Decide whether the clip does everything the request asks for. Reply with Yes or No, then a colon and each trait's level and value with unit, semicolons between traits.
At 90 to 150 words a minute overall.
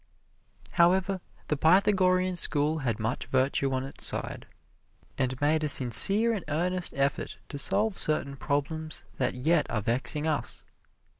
Yes: average, 140 wpm